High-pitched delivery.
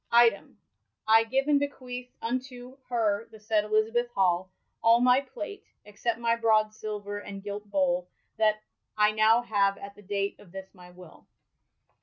Yes: high, 215 Hz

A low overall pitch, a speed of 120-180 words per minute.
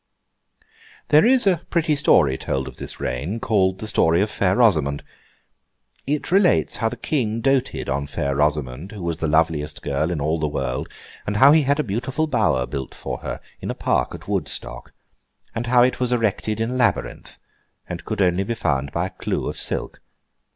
No: low, 100 Hz; average, 195 wpm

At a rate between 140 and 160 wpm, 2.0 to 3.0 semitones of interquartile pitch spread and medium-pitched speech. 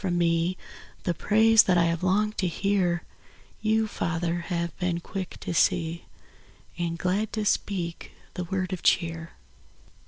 Yes: average, 150 wpm; narrow, 2.6 semitones; medium, 180 Hz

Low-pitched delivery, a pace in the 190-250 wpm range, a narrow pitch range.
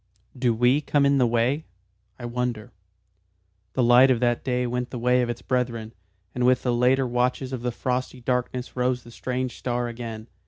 Yes: low, 125 Hz; average, 195 wpm; narrow, 1.2 semitones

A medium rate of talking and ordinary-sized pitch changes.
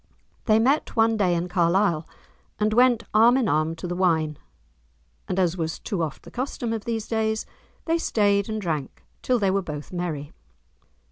Yes: average, 180 wpm; average, 4.8 semitones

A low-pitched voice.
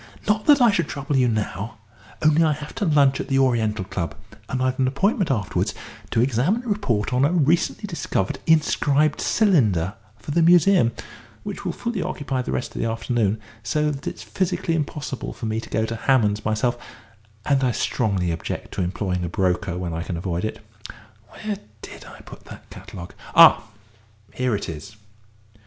Yes: low, 130 Hz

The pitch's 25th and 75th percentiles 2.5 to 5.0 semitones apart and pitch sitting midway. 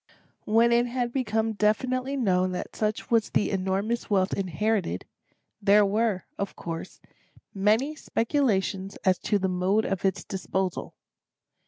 No: average, 3.3 semitones; high, 210 Hz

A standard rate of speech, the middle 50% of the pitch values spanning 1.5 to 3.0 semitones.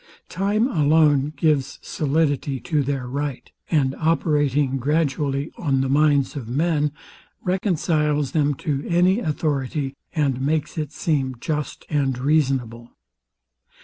No: slow, 115 wpm; narrow, 2.6 semitones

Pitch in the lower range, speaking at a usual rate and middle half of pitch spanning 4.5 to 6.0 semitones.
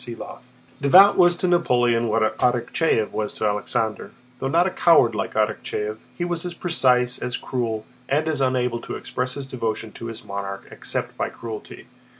Yes: low, 125 Hz; average, 170 wpm; average, 5.3 semitones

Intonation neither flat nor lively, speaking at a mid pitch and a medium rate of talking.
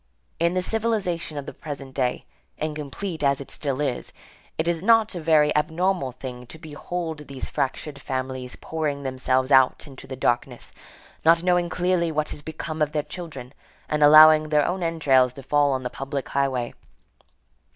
Yes: average, 3.8 semitones; medium, 150 Hz; average, 170 wpm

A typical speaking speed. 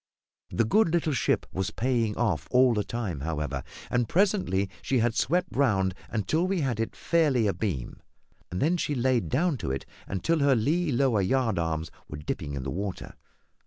Yes: average, 170 wpm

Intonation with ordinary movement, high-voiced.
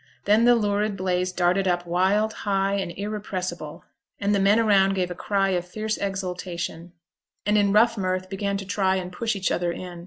No: narrow, 2.2 semitones; high, 195 Hz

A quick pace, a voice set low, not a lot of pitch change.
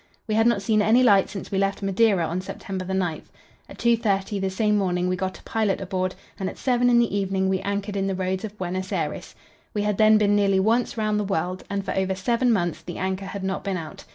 No: fast, 240 wpm; high, 195 Hz; narrow, 2.1 semitones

